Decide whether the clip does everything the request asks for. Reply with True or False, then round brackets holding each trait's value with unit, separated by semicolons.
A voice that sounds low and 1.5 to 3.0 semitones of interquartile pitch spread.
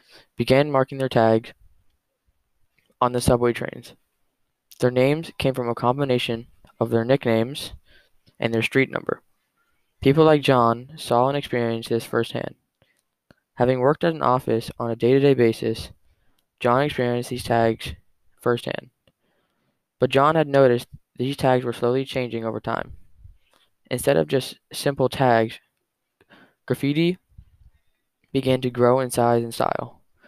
True (120 Hz; 2.5 semitones)